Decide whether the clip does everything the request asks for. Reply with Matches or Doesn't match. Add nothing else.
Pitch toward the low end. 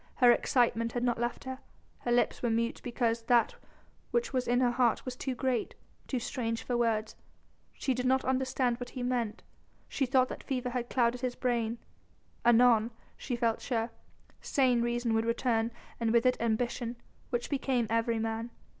Doesn't match